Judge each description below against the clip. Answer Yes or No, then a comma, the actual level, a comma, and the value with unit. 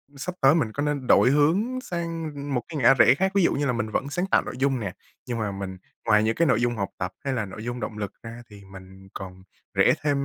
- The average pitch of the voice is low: Yes, low, 125 Hz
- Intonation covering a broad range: Yes, wide, 5.8 semitones